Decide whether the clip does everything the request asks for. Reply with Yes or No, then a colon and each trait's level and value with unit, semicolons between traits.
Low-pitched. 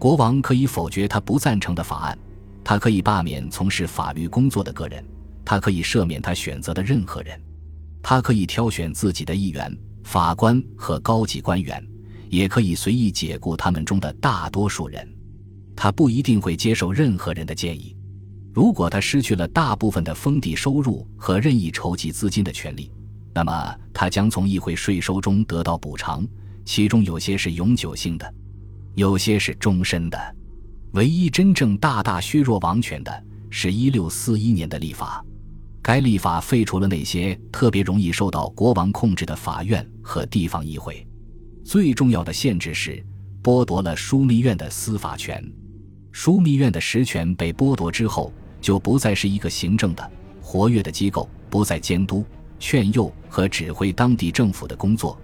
Yes: low, 100 Hz